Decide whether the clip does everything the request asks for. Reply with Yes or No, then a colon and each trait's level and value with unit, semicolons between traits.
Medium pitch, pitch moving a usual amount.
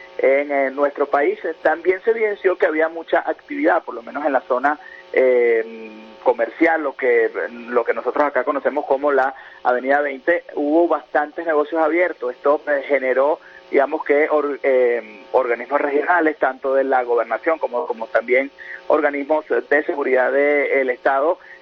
Yes: medium, 145 Hz; average, 4.1 semitones